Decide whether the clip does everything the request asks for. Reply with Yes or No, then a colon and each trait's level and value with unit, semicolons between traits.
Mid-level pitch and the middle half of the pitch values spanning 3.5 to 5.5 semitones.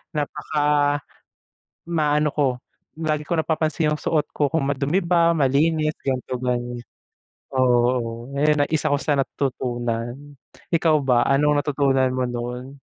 No: medium, 145 Hz; average, 3.1 semitones